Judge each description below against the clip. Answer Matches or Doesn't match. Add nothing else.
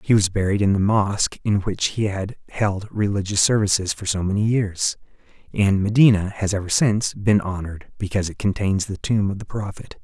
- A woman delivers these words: Doesn't match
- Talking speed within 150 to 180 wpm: Doesn't match